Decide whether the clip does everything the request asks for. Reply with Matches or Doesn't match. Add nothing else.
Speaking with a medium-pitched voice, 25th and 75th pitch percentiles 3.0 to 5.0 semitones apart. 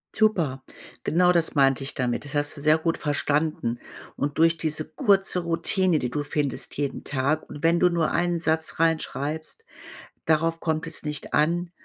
Doesn't match